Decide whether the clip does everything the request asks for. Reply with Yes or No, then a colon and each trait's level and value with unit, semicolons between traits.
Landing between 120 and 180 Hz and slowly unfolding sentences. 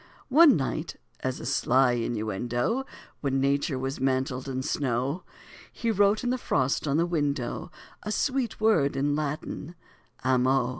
No: medium, 140 Hz; average, 145 wpm